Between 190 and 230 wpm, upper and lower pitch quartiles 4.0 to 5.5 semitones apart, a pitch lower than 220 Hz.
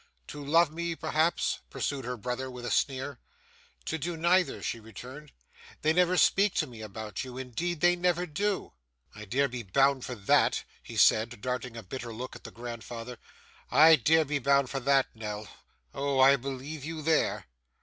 No: average, 180 wpm; average, 4.7 semitones; low, 135 Hz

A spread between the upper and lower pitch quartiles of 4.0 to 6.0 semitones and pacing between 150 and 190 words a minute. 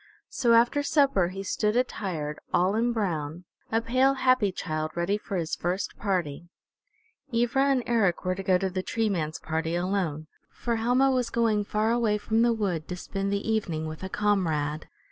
Yes: average, 5.1 semitones; average, 185 wpm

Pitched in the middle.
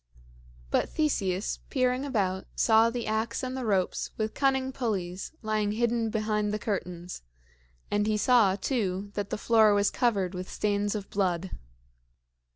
No: high, 210 Hz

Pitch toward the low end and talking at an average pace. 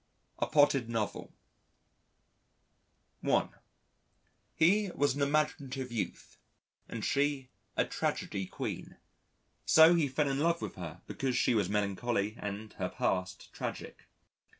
No: low, 130 Hz; slow, 120 wpm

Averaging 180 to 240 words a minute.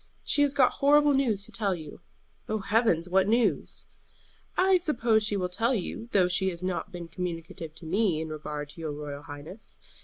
Yes: average, 190 wpm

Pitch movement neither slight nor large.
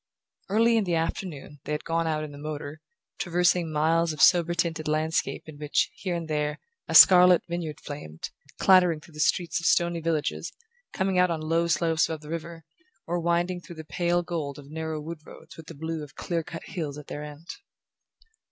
No: narrow, 2.1 semitones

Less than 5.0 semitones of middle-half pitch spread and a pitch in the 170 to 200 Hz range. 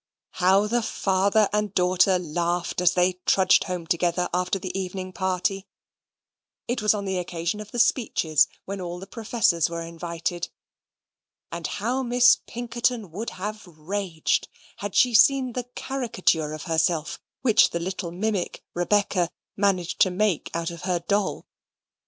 Yes: average, 3.4 semitones; medium, 185 Hz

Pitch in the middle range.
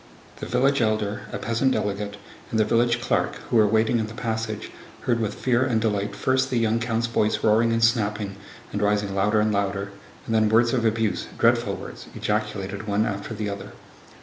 No: low, 110 Hz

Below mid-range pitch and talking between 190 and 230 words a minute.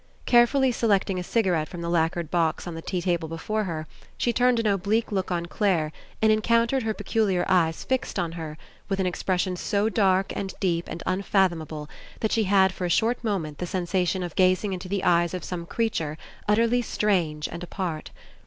No: medium, 185 Hz; average, 200 wpm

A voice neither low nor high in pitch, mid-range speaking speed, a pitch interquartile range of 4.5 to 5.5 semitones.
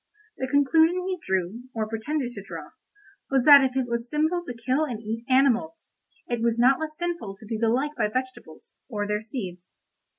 No: very high, 250 Hz; average, 195 wpm; average, 4.9 semitones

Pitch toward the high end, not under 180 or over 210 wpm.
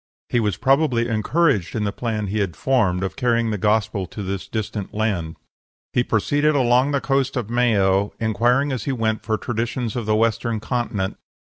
No: low, 115 Hz; average, 185 wpm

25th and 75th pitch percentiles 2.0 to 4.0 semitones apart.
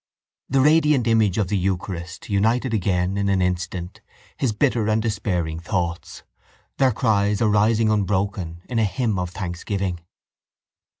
Yes: average, 3.5 semitones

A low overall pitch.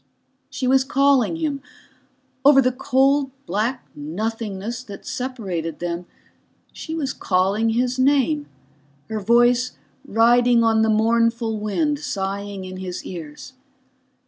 No: high, 230 Hz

